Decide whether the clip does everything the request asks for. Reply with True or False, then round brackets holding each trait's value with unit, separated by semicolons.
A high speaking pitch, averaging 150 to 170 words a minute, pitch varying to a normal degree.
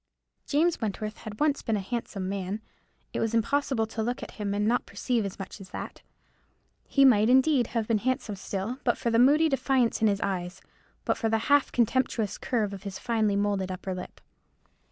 False (220 Hz; 195 wpm; 4.0 semitones)